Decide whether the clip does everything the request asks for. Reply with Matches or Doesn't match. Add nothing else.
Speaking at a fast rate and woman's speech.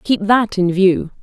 Doesn't match